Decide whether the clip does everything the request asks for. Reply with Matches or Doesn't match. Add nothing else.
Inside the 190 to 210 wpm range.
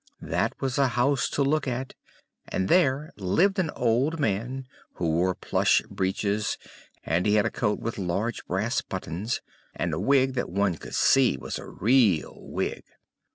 Doesn't match